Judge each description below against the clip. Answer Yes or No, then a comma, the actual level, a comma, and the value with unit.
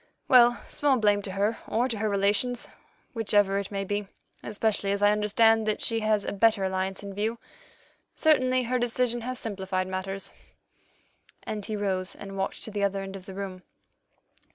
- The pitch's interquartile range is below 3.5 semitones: Yes, narrow, 2.5 semitones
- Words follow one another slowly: No, average, 175 wpm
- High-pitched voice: Yes, high, 205 Hz